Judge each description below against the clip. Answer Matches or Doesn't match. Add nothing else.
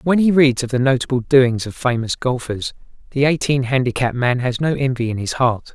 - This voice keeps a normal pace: Doesn't match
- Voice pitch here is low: Matches